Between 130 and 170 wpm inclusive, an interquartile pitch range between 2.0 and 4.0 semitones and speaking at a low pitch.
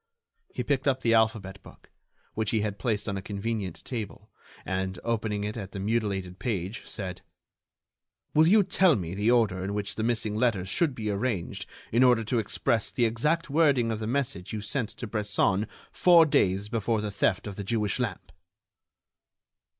No: average, 180 wpm; average, 3.3 semitones; low, 110 Hz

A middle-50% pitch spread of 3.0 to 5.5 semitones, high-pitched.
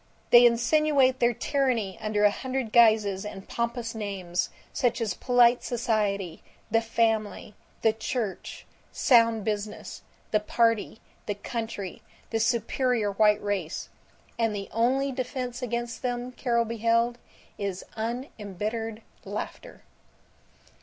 No: narrow, 2.6 semitones; high, 230 Hz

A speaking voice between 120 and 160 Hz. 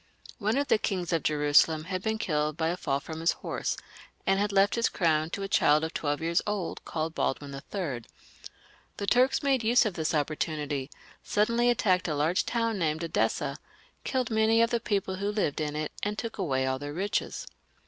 No: medium, 175 Hz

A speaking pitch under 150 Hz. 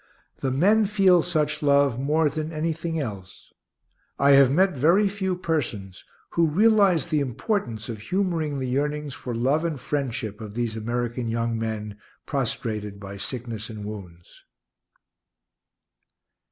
Yes: medium, 140 Hz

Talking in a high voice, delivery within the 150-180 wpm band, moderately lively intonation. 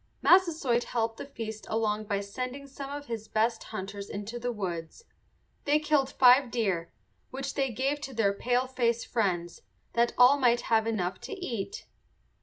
Yes: high, 235 Hz; average, 160 wpm; average, 4.1 semitones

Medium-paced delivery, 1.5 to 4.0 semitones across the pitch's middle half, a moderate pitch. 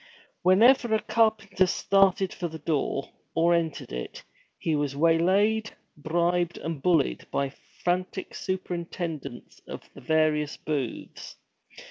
No: slow, 120 wpm; average, 3.4 semitones; medium, 170 Hz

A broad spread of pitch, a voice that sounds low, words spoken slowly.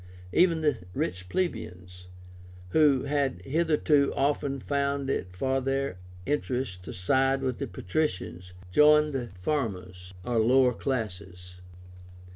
Yes: wide, 7.6 semitones; low, 130 Hz; slow, 115 wpm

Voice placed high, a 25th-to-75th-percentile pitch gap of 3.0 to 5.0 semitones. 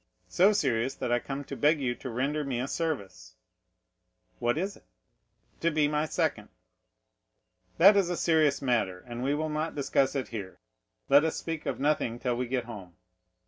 No: medium, 140 Hz; average, 4.4 semitones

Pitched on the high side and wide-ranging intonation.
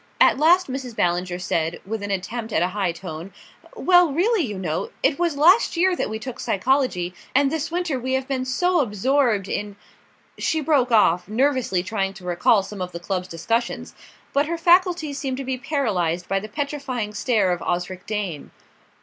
Yes: high, 230 Hz; wide, 7.3 semitones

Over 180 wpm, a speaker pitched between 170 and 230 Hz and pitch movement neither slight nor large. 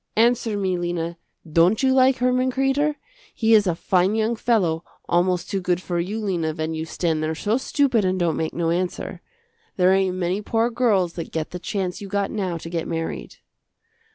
Yes: average, 195 wpm; medium, 185 Hz; average, 4.6 semitones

